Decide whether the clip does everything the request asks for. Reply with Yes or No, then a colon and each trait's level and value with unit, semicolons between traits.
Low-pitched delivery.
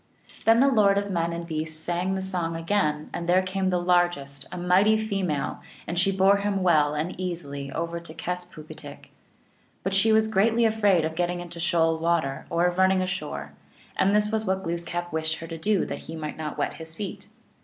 No: medium, 175 Hz